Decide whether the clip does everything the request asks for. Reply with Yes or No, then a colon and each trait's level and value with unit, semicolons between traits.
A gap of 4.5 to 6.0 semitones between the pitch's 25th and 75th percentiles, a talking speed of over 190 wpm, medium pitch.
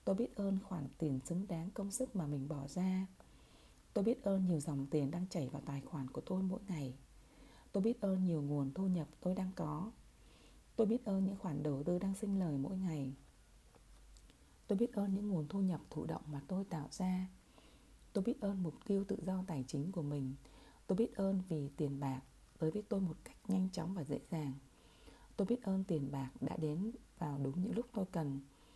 Yes: average, 5.2 semitones; average, 215 wpm; medium, 180 Hz